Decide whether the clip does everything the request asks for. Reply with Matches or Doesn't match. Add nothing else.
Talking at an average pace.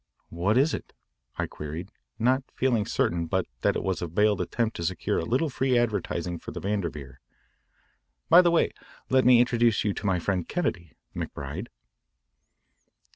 Matches